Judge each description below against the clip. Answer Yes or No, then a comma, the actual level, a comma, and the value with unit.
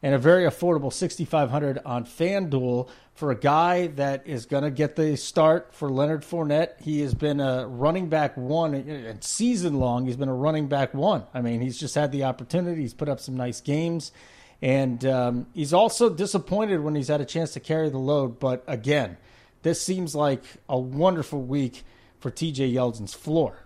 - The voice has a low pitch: No, medium, 145 Hz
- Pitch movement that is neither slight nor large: Yes, average, 3.8 semitones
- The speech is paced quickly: No, average, 190 wpm